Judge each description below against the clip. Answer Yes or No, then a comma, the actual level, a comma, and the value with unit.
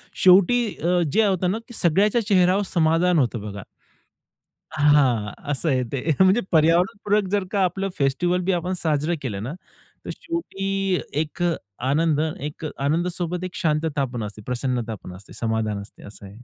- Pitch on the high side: No, medium, 160 Hz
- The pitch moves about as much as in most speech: No, wide, 6.1 semitones